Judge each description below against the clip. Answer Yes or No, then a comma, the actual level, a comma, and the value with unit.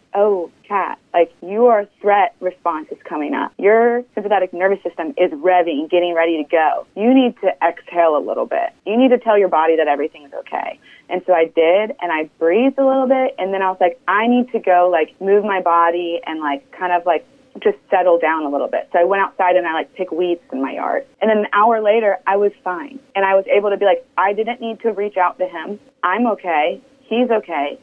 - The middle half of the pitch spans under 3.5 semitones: No, average, 4.7 semitones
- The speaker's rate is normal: No, fast, 235 wpm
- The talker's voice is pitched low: No, high, 195 Hz